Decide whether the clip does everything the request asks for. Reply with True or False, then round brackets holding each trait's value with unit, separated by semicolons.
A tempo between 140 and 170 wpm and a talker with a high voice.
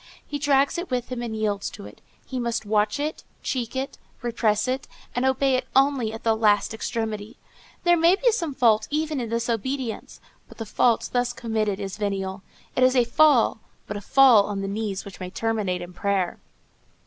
False (195 wpm; 230 Hz)